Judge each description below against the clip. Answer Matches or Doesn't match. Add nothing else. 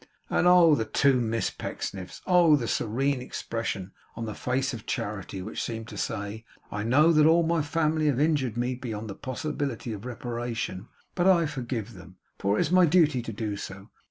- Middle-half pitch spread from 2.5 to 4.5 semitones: Doesn't match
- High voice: Doesn't match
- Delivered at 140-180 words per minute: Doesn't match